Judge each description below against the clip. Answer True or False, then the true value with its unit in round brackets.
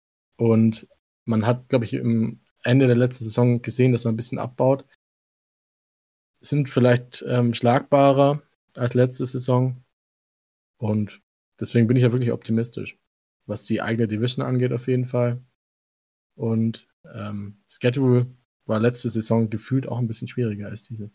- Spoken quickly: False (145 wpm)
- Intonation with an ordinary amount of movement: False (1.9 semitones)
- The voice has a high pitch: False (120 Hz)